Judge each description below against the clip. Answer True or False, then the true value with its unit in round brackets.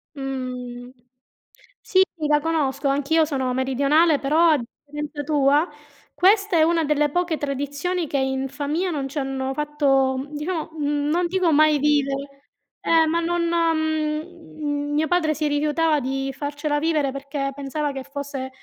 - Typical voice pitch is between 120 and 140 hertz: False (295 Hz)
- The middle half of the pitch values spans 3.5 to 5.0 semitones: False (2.5 semitones)